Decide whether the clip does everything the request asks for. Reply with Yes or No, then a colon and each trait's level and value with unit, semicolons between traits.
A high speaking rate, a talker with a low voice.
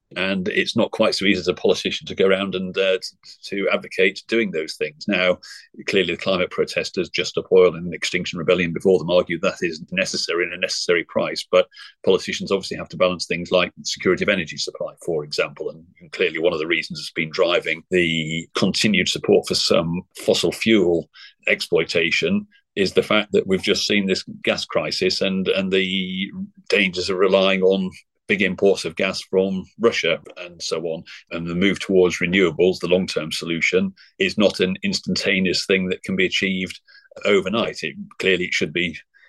No: average, 190 wpm; low, 100 Hz